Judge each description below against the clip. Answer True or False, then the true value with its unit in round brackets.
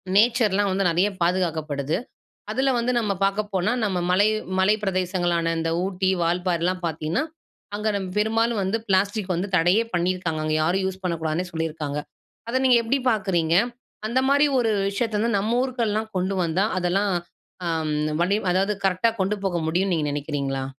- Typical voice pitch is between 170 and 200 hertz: True (190 Hz)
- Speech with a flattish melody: False (3.7 semitones)